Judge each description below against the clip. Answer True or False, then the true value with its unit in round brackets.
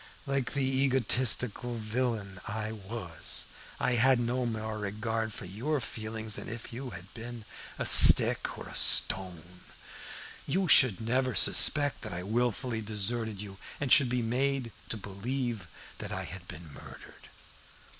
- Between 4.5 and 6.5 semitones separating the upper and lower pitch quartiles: False (3.3 semitones)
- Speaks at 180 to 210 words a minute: False (150 wpm)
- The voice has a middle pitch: False (115 Hz)